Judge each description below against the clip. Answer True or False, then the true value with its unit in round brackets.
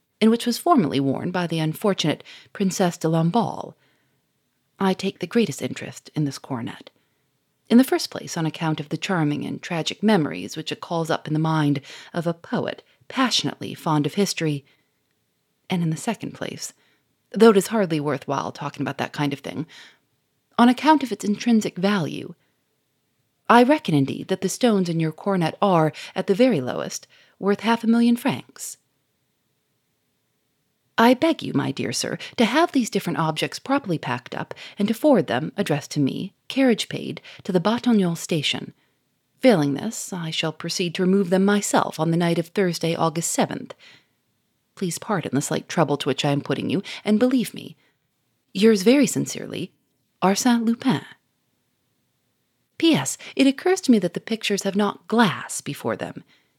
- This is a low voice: False (180 Hz)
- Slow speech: False (175 wpm)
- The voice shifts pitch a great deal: True (6.8 semitones)